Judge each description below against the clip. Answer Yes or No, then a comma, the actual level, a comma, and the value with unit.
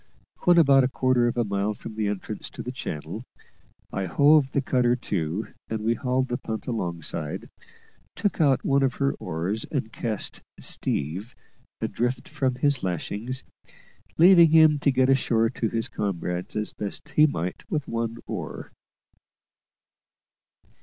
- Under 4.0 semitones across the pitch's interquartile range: No, average, 4.6 semitones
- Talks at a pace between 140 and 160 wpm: Yes, average, 150 wpm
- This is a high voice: No, low, 120 Hz